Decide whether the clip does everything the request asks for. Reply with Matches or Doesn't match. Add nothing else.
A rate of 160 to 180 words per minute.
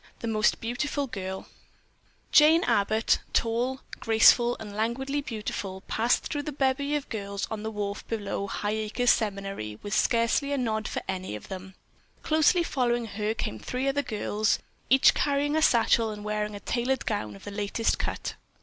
Matches